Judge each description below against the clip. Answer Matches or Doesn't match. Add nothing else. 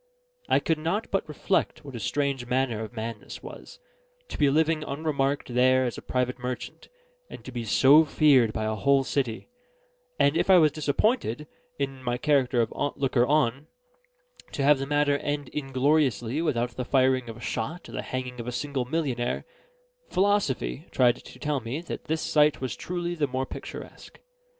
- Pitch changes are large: Doesn't match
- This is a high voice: Doesn't match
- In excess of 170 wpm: Matches